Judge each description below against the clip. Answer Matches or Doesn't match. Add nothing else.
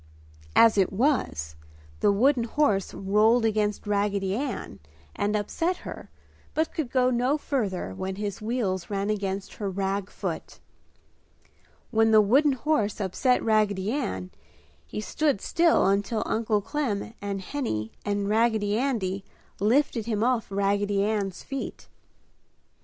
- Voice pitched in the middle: Doesn't match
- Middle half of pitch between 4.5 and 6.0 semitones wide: Doesn't match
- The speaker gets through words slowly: Matches